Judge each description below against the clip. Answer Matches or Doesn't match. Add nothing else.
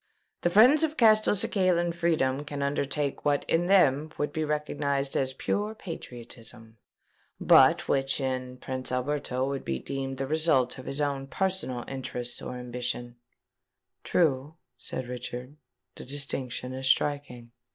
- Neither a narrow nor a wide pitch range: Matches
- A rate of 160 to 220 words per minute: Doesn't match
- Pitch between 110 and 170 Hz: Matches